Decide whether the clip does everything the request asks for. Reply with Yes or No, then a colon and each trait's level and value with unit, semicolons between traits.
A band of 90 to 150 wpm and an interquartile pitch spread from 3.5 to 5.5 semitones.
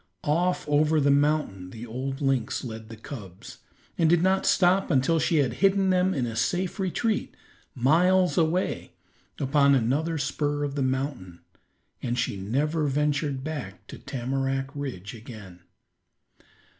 Yes: average, 145 wpm; average, 4.6 semitones